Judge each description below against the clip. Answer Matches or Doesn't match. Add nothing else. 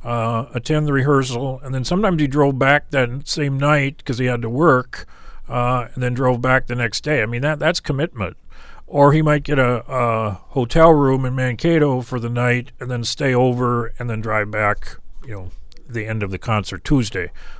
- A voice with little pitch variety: Doesn't match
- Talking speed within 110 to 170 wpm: Doesn't match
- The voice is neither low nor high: Doesn't match